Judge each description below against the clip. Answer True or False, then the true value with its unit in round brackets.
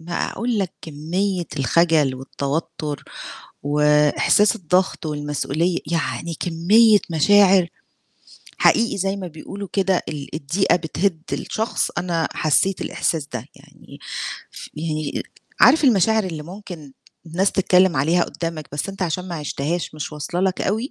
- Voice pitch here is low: False (170 Hz)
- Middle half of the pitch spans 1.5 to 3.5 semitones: False (4.1 semitones)